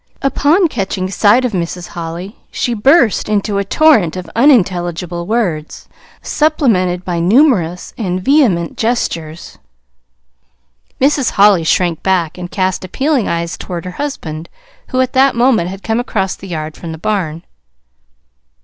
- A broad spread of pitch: Yes, wide, 6.1 semitones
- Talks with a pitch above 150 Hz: Yes, high, 190 Hz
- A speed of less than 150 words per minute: Yes, average, 140 wpm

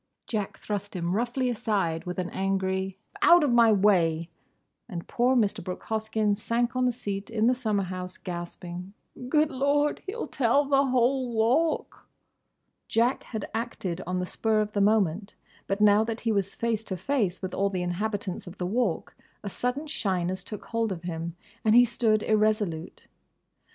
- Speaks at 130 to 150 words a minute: No, average, 170 wpm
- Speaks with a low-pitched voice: No, high, 210 Hz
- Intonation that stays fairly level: No, average, 4.3 semitones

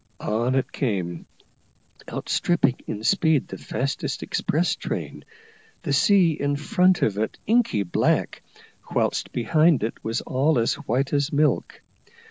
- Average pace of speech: No, slow, 130 wpm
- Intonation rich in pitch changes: Yes, wide, 5.7 semitones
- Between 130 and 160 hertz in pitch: Yes, medium, 140 Hz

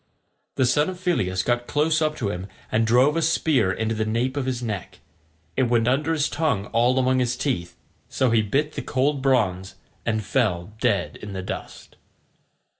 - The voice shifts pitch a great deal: No, average, 4.7 semitones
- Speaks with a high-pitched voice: No, low, 125 Hz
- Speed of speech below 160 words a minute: No, average, 190 wpm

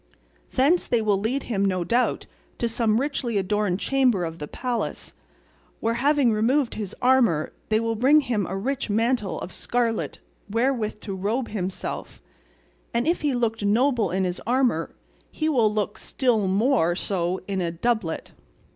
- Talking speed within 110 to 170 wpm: Yes, average, 160 wpm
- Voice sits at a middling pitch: No, high, 225 Hz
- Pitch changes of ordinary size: Yes, average, 4.4 semitones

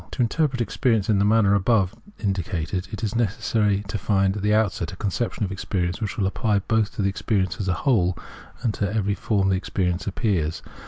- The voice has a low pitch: Yes, low, 100 Hz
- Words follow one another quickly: Yes, fast, 215 wpm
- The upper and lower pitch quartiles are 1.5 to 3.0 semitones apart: Yes, narrow, 2.6 semitones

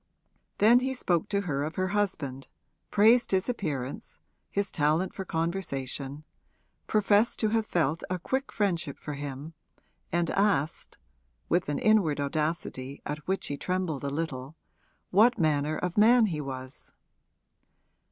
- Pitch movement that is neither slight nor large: No, wide, 5.9 semitones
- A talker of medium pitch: Yes, medium, 165 Hz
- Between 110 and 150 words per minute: Yes, average, 140 wpm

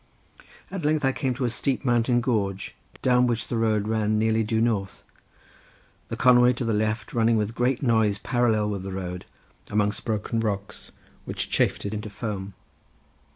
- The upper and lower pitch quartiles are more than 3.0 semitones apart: No, average, 2.7 semitones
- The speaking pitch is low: Yes, low, 110 Hz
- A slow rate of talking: No, average, 175 wpm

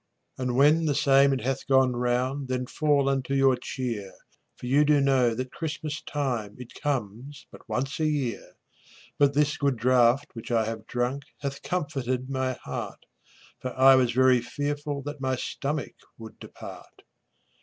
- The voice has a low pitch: Yes, low, 130 Hz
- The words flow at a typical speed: Yes, average, 165 wpm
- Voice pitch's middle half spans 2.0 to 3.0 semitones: Yes, narrow, 2.4 semitones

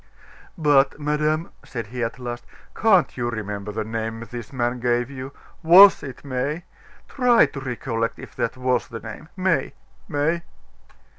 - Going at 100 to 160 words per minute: Yes, average, 150 wpm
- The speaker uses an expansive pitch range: No, average, 4.5 semitones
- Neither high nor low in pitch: No, low, 130 Hz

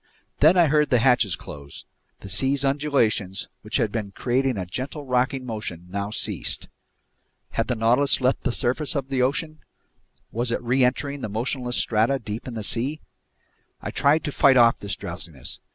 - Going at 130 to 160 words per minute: No, average, 170 wpm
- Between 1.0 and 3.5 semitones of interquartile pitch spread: No, average, 4.3 semitones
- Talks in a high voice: No, low, 125 Hz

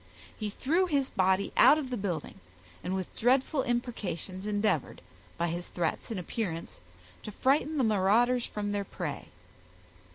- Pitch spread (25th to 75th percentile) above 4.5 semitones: Yes, average, 5.2 semitones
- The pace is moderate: Yes, average, 150 wpm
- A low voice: No, high, 210 Hz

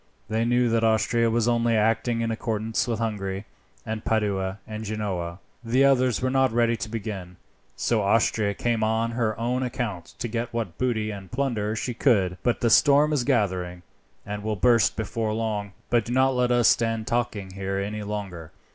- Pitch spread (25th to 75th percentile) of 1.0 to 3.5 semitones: Yes, narrow, 2.5 semitones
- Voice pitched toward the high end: No, low, 110 Hz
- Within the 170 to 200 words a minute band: Yes, average, 180 wpm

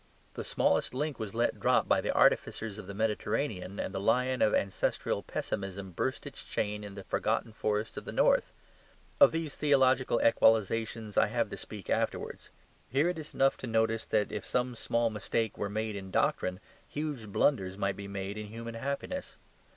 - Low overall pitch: Yes, low, 110 Hz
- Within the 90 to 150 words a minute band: No, average, 180 wpm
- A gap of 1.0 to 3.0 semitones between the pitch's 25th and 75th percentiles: No, average, 4.1 semitones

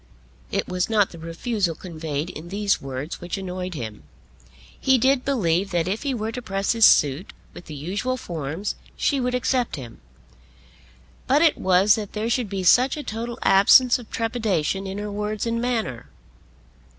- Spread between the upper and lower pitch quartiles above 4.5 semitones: Yes, wide, 5.5 semitones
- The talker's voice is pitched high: Yes, high, 200 Hz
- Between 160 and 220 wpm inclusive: Yes, average, 175 wpm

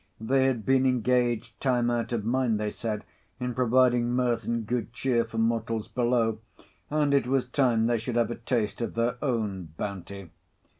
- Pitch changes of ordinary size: No, narrow, 2.0 semitones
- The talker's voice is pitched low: Yes, low, 120 Hz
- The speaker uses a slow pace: No, average, 180 wpm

